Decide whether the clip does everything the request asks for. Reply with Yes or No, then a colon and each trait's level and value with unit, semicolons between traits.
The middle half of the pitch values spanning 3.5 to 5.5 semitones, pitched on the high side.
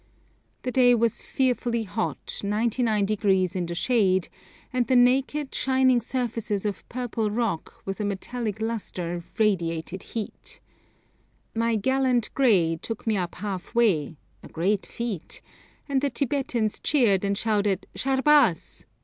Yes: average, 4.1 semitones; high, 220 Hz